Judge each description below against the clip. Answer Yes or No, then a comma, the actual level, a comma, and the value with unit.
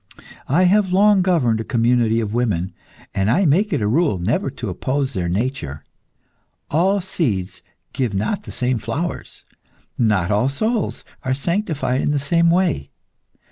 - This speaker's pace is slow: No, average, 155 wpm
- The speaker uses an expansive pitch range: Yes, wide, 7.9 semitones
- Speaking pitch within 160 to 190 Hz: No, low, 130 Hz